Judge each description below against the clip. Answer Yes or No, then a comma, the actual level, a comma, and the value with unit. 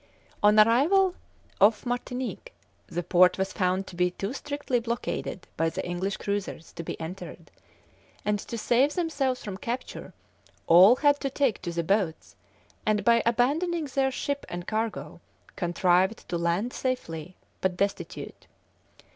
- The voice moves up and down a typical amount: No, wide, 6.1 semitones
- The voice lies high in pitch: Yes, high, 210 Hz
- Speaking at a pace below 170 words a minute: Yes, average, 145 wpm